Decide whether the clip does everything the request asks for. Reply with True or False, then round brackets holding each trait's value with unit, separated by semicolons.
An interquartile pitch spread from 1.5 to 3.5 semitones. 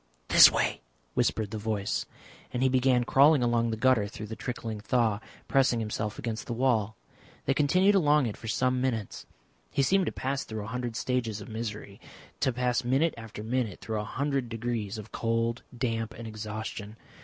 True (2.8 semitones)